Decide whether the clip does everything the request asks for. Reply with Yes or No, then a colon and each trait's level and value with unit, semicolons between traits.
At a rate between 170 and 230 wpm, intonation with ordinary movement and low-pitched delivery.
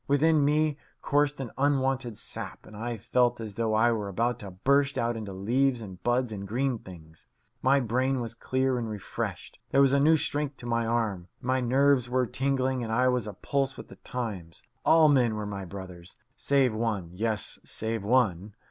Yes: average, 190 wpm; average, 3.9 semitones; low, 120 Hz